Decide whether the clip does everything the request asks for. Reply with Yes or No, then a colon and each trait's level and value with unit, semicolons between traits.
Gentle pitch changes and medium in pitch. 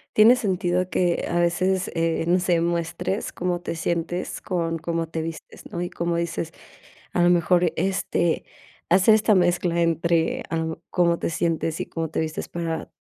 Yes: narrow, 1.5 semitones; medium, 170 Hz